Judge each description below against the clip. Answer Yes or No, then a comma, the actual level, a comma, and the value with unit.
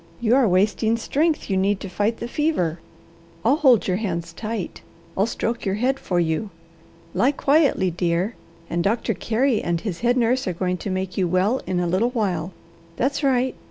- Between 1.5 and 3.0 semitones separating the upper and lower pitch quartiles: No, average, 5.2 semitones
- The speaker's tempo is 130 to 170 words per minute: No, average, 190 wpm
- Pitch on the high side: Yes, high, 210 Hz